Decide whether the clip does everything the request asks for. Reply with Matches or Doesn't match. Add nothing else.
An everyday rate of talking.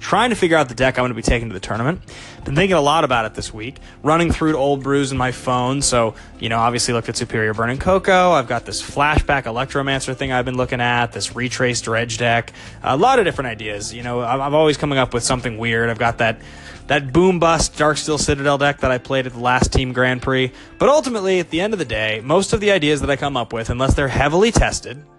Doesn't match